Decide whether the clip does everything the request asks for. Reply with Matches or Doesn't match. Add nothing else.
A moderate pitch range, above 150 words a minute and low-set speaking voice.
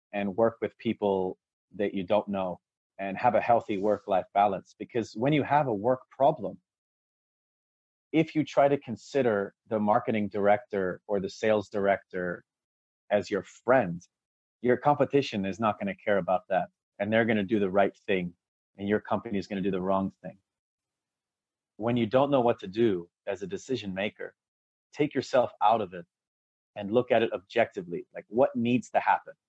Matches